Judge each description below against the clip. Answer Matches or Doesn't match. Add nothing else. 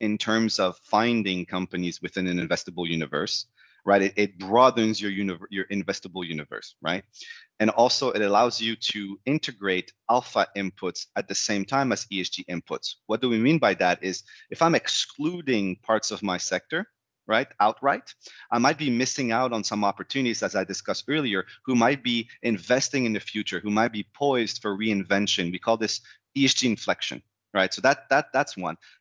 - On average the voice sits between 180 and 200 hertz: Doesn't match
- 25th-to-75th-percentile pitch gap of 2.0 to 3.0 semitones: Doesn't match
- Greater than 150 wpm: Matches